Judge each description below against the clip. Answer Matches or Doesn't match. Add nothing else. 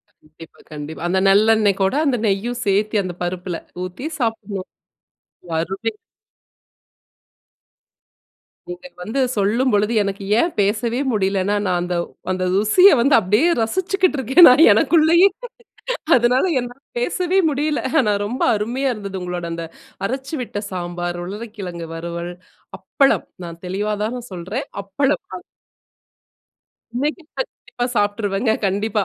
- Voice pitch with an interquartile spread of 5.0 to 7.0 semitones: Matches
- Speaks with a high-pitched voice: Matches